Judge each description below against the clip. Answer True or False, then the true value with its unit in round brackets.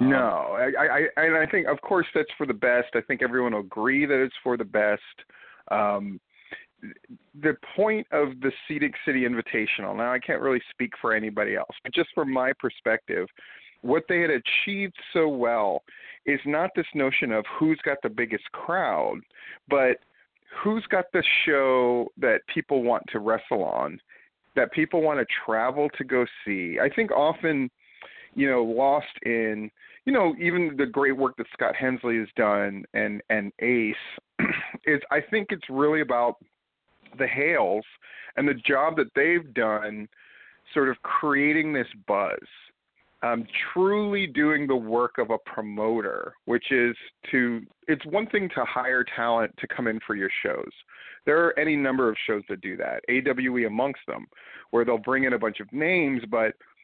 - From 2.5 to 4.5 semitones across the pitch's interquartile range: False (4.9 semitones)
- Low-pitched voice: True (130 Hz)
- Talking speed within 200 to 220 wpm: False (170 wpm)